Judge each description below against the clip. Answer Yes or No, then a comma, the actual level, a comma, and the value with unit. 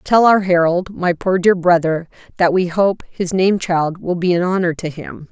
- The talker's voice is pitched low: No, medium, 180 Hz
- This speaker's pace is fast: No, average, 190 wpm